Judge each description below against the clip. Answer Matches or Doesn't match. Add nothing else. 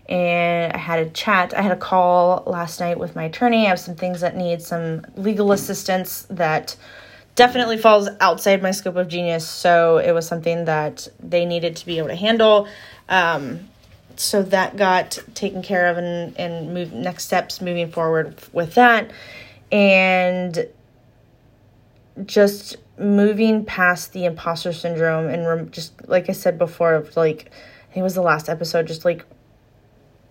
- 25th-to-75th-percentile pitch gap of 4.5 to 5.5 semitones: Doesn't match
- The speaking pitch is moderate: Matches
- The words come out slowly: Doesn't match